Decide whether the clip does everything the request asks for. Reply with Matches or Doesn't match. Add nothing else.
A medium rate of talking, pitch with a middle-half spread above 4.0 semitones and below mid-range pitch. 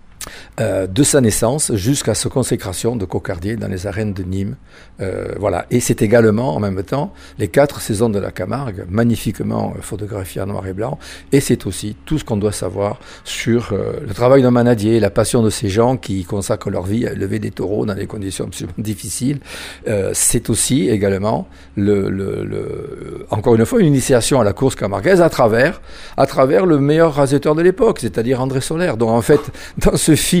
Matches